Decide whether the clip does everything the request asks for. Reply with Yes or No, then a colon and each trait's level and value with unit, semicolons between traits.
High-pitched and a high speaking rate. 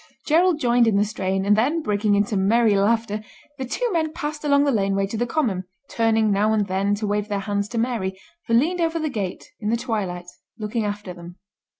Yes: high, 215 Hz; fast, 215 wpm